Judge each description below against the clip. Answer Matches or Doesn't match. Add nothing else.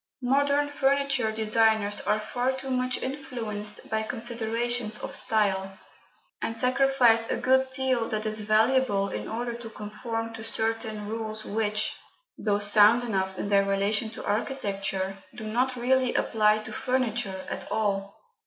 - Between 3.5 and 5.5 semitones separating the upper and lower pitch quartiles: Doesn't match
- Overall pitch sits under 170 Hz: Doesn't match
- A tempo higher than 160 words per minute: Doesn't match